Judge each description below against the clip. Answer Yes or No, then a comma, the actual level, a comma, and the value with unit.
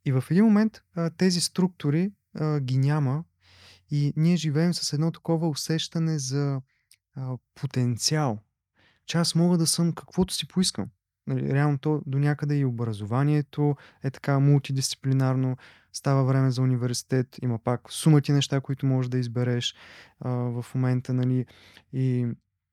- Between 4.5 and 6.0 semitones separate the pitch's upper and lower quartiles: No, average, 3.6 semitones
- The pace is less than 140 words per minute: No, average, 145 wpm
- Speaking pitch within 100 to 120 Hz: No, low, 135 Hz